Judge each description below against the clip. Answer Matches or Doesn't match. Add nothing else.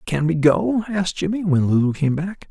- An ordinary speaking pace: Doesn't match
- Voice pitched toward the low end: Doesn't match